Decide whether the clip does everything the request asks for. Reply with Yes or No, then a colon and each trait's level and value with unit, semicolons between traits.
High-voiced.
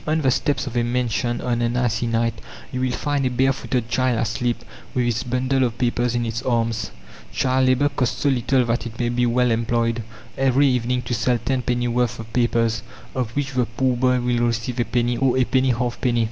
No: low, 120 Hz